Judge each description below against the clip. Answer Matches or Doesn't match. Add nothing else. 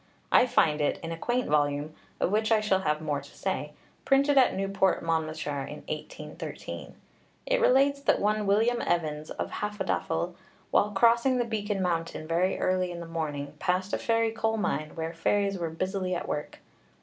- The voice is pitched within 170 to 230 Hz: Matches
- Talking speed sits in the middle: Matches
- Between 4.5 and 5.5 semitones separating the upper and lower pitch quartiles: Matches